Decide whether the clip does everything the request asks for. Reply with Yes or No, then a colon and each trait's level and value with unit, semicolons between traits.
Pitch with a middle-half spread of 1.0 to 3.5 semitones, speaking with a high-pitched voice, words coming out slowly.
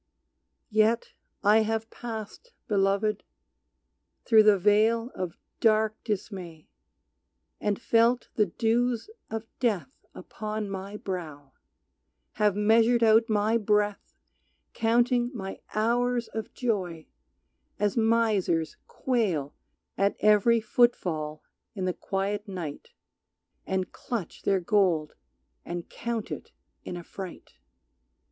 Yes: average, 3.0 semitones; high, 210 Hz; slow, 105 wpm